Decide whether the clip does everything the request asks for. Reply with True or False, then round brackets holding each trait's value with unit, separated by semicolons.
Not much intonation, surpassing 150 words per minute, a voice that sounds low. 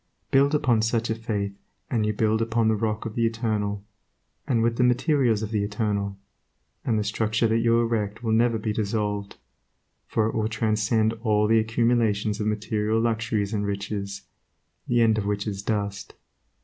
True (1.6 semitones; 175 wpm; 110 Hz)